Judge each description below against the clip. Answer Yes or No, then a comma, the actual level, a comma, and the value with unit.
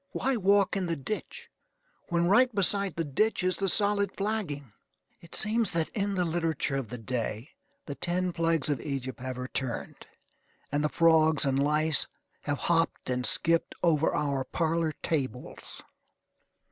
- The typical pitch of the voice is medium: Yes, medium, 165 Hz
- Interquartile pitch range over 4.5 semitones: Yes, average, 5.1 semitones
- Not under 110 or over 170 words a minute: Yes, average, 155 wpm